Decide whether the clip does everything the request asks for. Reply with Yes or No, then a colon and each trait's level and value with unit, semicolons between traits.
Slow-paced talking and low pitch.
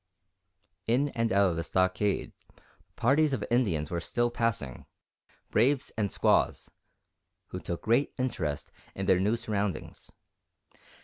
Yes: slow, 125 wpm; low, 105 Hz